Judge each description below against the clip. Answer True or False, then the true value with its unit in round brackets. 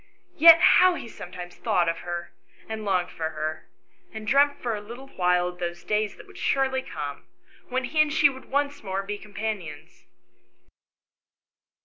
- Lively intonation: True (7.0 semitones)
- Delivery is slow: False (165 wpm)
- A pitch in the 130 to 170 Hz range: False (210 Hz)